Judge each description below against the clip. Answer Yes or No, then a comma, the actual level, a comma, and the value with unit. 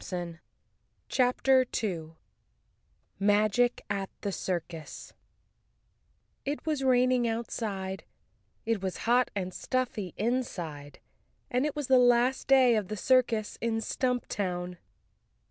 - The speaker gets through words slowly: Yes, slow, 110 wpm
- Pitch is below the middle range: No, high, 225 Hz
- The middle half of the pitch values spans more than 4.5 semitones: Yes, average, 4.9 semitones